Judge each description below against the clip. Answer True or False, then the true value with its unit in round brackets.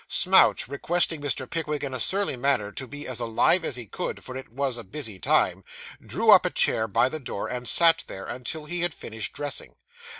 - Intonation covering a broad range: False (4.3 semitones)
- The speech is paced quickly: True (210 wpm)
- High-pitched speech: False (130 Hz)